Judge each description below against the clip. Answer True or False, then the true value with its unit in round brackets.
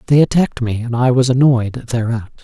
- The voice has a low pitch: True (125 Hz)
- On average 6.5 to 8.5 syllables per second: False (5.6 syllables/s)